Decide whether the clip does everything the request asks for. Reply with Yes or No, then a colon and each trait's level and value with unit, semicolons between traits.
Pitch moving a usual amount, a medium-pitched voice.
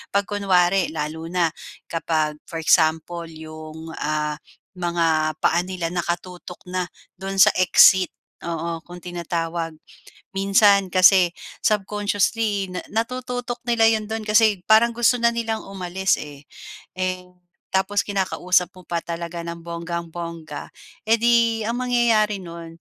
Yes: average, 3.9 semitones; medium, 180 Hz